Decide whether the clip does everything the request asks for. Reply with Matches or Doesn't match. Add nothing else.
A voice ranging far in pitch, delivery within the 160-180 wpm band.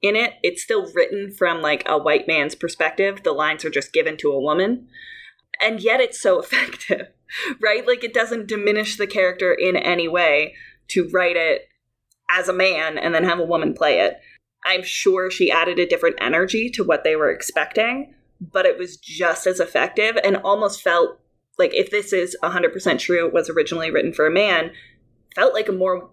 Doesn't match